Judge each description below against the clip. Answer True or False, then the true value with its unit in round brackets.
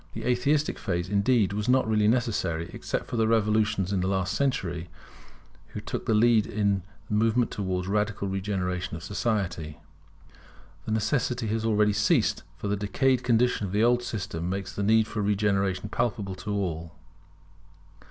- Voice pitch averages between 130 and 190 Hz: False (105 Hz)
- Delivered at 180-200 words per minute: False (160 wpm)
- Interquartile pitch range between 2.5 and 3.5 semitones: True (2.9 semitones)